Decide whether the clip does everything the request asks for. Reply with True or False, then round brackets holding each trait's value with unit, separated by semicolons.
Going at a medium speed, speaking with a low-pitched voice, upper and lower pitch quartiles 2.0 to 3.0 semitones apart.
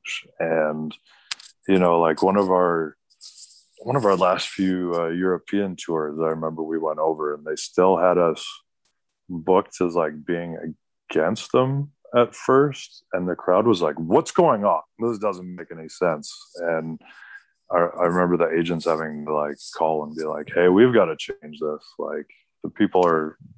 True (175 wpm; 85 Hz; 2.7 semitones)